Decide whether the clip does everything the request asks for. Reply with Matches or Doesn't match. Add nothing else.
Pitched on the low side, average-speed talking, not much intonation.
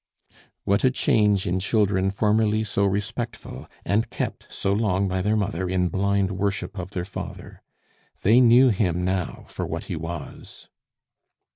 Matches